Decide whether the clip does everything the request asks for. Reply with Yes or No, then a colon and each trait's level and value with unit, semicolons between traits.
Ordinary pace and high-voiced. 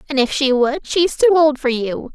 No: fast, 280 wpm; very high, 285 Hz